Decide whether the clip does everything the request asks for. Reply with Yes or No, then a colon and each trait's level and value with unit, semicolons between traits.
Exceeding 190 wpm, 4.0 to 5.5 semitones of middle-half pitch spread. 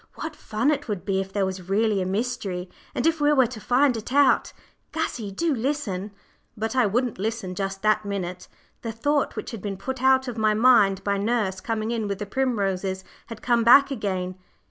Yes: fast, 205 wpm; average, 4.4 semitones